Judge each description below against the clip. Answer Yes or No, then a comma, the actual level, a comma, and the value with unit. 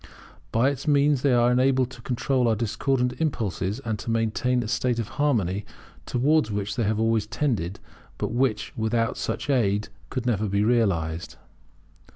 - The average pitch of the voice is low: Yes, low, 115 Hz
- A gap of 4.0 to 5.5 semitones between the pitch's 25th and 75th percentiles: No, average, 3.3 semitones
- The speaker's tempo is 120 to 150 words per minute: No, average, 165 wpm